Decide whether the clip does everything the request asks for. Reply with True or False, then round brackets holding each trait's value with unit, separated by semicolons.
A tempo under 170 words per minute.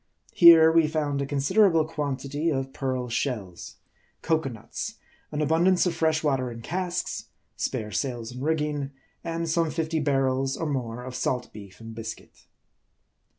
True (150 wpm)